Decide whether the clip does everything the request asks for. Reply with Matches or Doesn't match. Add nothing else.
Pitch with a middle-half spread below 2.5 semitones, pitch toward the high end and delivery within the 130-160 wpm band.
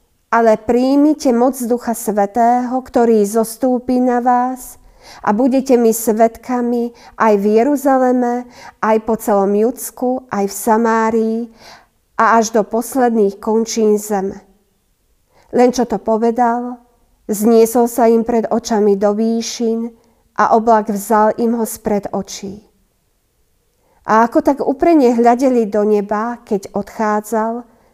Doesn't match